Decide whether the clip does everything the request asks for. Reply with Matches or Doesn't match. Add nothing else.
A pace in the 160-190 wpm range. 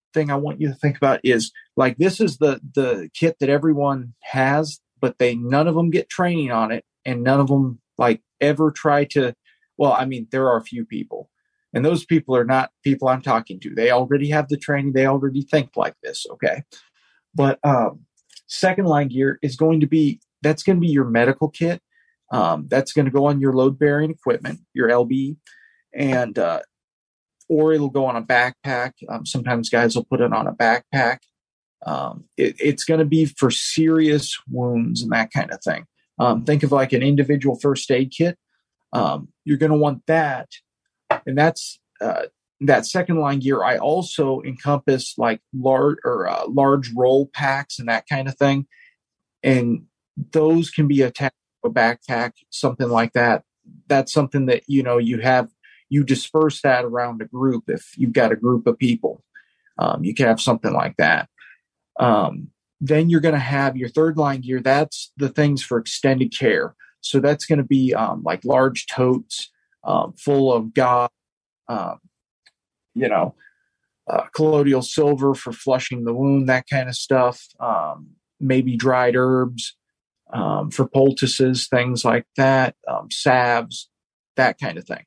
Matches